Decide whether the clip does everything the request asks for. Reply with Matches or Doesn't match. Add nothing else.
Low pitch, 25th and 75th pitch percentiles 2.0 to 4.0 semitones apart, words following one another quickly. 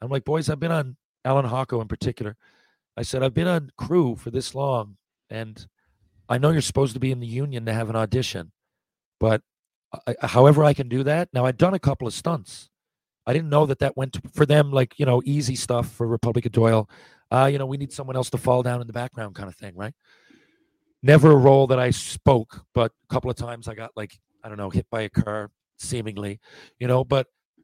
Matches